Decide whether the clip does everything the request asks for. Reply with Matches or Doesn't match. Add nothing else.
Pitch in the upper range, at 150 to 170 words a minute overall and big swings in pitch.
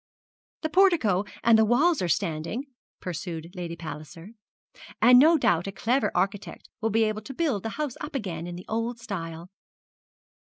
Matches